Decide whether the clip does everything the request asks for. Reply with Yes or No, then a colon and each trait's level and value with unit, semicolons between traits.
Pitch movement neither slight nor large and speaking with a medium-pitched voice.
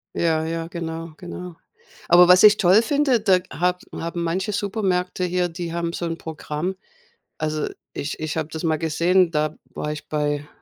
No: narrow, 2.3 semitones; medium, 170 Hz